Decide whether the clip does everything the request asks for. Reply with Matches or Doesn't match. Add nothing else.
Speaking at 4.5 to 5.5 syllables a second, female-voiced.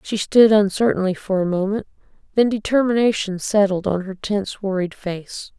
Matches